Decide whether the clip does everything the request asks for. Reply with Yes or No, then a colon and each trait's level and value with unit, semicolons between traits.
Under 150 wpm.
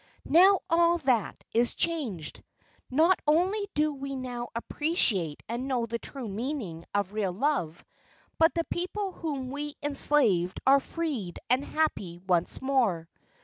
Yes: average, 140 wpm